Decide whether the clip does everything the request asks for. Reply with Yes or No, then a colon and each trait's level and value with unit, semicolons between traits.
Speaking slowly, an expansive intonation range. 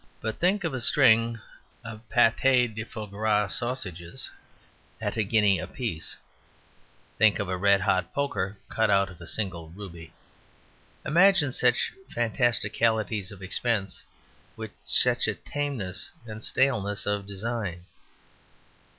No: slow, 130 wpm; average, 3.6 semitones